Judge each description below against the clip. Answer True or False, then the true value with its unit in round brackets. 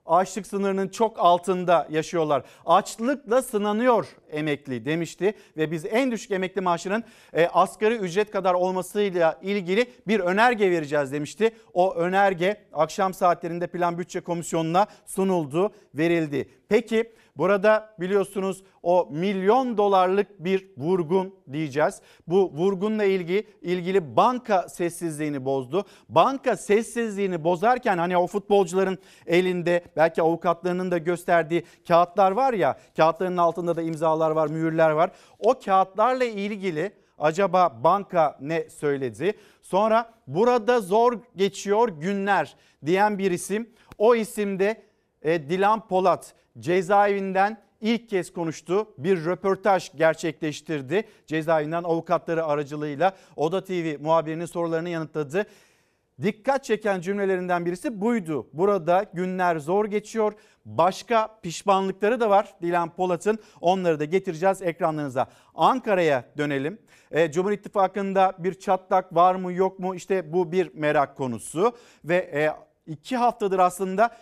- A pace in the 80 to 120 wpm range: True (115 wpm)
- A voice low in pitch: False (185 Hz)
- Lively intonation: False (3.5 semitones)